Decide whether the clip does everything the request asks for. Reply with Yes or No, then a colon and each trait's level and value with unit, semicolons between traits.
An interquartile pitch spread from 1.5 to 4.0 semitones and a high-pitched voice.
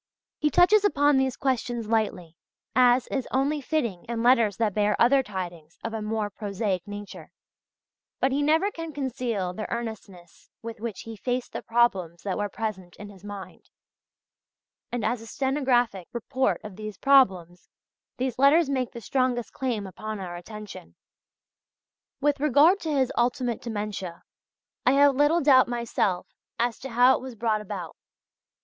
No: average, 4.4 semitones; high, 235 Hz